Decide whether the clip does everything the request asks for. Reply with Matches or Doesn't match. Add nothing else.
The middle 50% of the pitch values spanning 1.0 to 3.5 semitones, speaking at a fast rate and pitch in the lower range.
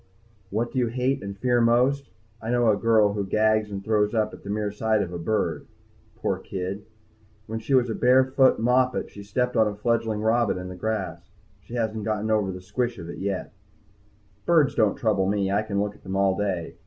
Matches